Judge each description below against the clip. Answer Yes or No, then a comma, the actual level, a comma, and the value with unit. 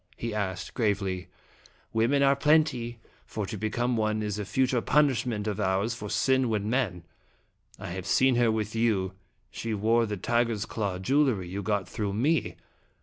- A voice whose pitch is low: Yes, low, 110 Hz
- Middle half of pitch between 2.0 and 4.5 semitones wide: Yes, average, 3.2 semitones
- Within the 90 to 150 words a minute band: No, average, 170 wpm